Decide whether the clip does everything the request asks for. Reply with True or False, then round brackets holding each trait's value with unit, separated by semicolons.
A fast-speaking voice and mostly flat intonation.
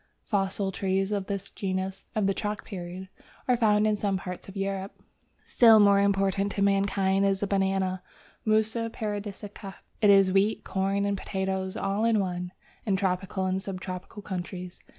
False (165 wpm; 1.3 semitones)